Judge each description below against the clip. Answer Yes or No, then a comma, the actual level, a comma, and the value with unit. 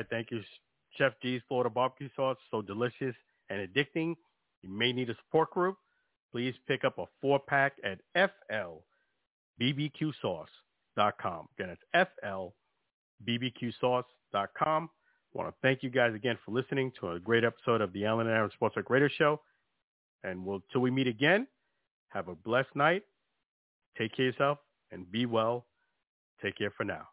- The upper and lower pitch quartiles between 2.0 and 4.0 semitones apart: Yes, average, 3.5 semitones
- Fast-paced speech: No, average, 155 wpm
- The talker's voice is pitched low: Yes, low, 125 Hz